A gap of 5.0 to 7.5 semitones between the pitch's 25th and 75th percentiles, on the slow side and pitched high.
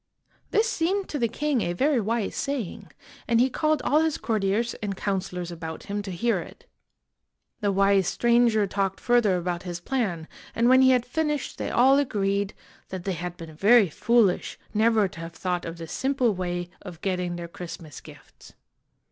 No: wide, 5.4 semitones; average, 180 wpm; high, 200 Hz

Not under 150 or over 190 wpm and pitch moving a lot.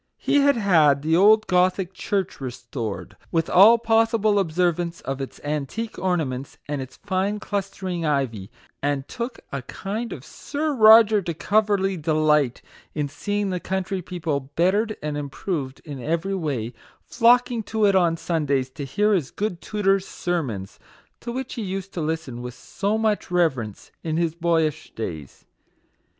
Yes: average, 155 wpm; wide, 5.9 semitones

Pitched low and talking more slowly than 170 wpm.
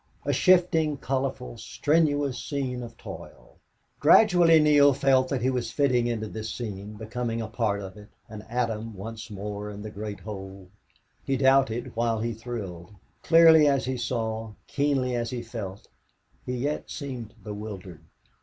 Yes: low, 120 Hz; average, 155 wpm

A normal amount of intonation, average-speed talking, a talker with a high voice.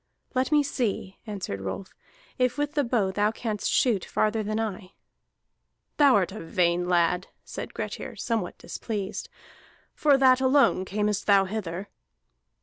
Yes: average, 5.0 semitones; average, 145 wpm; high, 210 Hz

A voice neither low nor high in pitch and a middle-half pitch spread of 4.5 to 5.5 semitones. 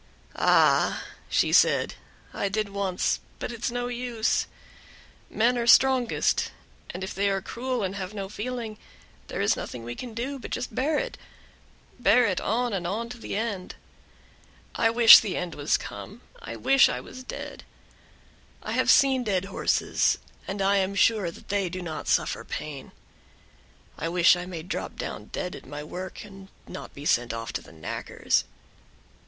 No: high, 200 Hz; average, 4.8 semitones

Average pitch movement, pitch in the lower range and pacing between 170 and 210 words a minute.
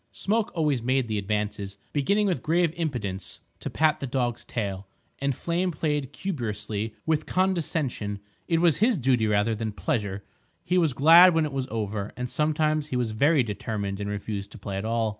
No: wide, 7.1 semitones; low, 130 Hz; average, 180 wpm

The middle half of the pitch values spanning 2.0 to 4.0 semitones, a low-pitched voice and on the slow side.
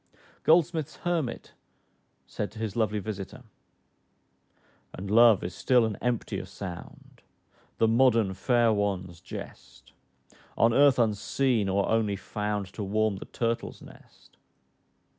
Yes: average, 3.2 semitones; low, 110 Hz; slow, 120 wpm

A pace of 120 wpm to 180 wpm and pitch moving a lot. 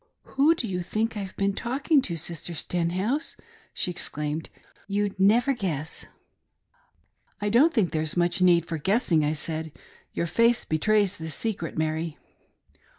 Yes: average, 160 wpm; wide, 5.8 semitones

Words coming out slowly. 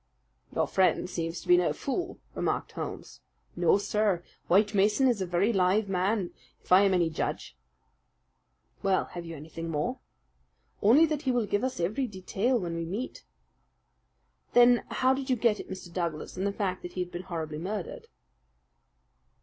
No: average, 175 wpm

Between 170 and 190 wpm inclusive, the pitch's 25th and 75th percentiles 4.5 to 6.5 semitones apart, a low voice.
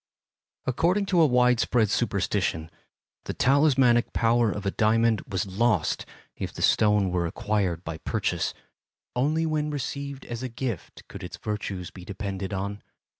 No: average, 150 wpm; average, 4.8 semitones; low, 110 Hz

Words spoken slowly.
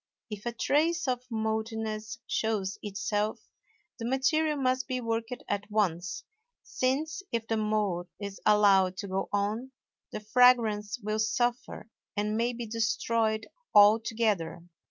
Yes: slow, 130 wpm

